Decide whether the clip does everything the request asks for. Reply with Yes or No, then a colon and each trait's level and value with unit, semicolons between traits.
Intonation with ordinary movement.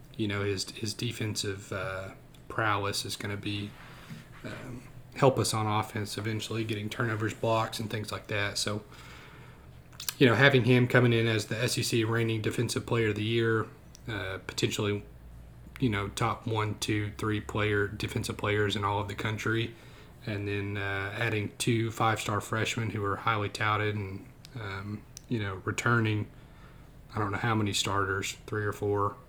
No: narrow, 2.3 semitones